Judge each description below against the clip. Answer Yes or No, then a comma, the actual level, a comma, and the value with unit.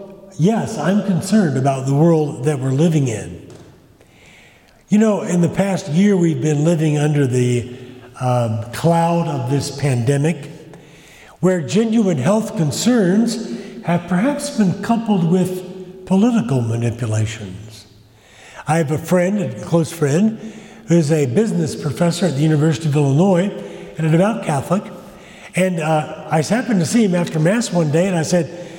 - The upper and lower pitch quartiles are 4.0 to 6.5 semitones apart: Yes, average, 4.6 semitones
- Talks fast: No, average, 150 wpm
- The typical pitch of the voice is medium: Yes, medium, 170 Hz